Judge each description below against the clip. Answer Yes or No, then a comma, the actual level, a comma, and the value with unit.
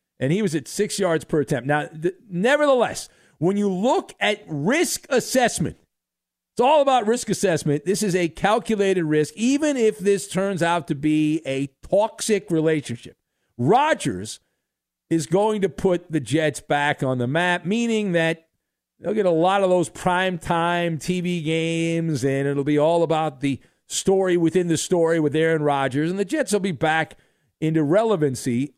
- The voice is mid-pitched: Yes, medium, 170 Hz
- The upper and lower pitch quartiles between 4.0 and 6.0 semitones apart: Yes, average, 4.4 semitones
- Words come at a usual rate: Yes, average, 165 wpm